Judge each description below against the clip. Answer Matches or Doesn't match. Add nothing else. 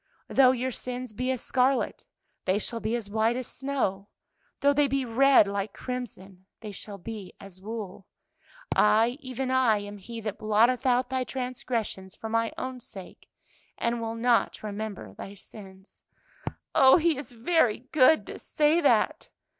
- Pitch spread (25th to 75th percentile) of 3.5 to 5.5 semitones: Matches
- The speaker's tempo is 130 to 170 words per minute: Matches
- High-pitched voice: Matches